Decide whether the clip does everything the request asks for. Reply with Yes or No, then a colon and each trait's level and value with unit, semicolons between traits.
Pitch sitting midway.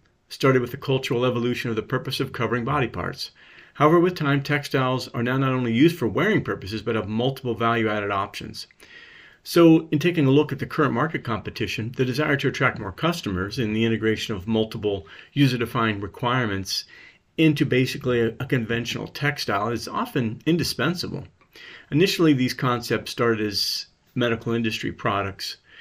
No: low, 125 Hz